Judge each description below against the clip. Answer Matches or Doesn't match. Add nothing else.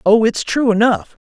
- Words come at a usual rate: Matches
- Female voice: Matches